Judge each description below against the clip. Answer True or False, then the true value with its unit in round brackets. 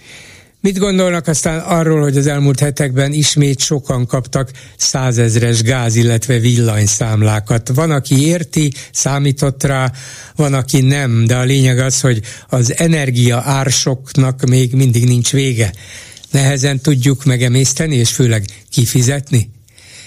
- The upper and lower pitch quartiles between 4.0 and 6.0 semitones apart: False (2.7 semitones)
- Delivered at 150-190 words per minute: False (125 wpm)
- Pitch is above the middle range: False (130 Hz)